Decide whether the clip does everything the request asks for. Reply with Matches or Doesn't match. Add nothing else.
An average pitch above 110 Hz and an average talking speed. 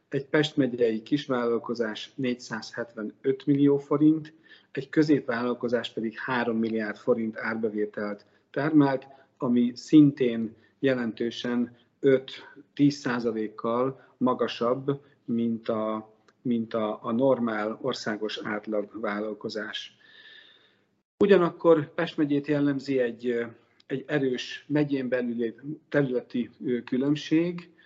Doesn't match